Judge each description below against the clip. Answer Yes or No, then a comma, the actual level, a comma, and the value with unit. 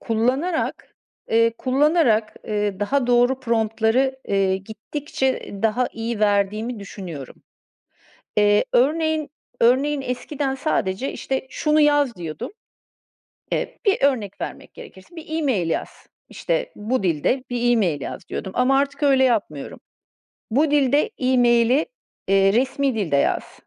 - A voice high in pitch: Yes, high, 245 Hz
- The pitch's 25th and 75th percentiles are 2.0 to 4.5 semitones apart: No, average, 5.0 semitones